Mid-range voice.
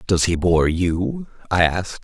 No: very low, 90 Hz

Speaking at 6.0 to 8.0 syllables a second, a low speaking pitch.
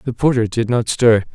No: 4.9 syllables/s; low, 115 Hz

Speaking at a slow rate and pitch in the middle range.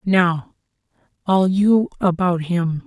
Yes: slow, 105 wpm; medium, 180 Hz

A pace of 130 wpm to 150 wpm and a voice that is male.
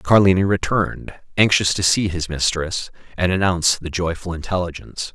Yes: average, 140 wpm; male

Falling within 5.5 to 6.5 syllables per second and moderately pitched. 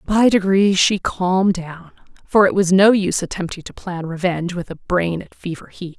No: 5.1 syllables/s; medium, 180 Hz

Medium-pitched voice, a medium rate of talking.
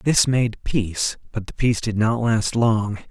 No: low, 110 Hz; average, 195 wpm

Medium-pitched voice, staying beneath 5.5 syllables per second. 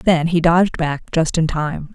Yes: medium, 165 Hz; 4.4 syllables/s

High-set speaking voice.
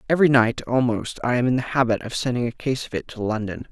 No: low, 125 Hz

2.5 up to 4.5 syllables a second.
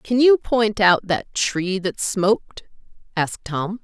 Yes: 3.7 syllables/s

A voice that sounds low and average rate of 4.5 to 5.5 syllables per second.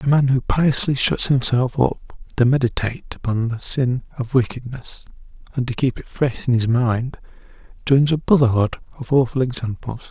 Yes: low, 125 Hz; 5.0 syllables/s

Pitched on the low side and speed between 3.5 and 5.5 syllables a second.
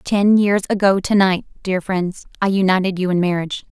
No: high, 190 Hz; 5.3 syllables/s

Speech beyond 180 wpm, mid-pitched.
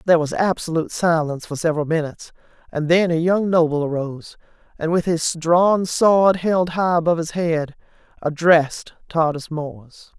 No: average, 155 wpm; medium, 165 Hz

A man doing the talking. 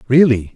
Yes: male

